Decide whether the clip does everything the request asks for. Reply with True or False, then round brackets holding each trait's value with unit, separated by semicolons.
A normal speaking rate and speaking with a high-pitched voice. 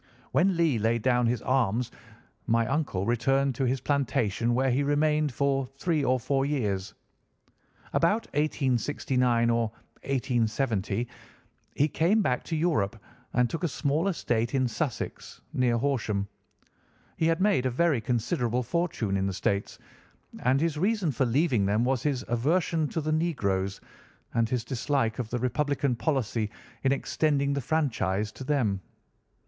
False (150 wpm; 130 Hz)